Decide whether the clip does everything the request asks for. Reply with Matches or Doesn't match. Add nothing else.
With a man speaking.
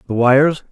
Matches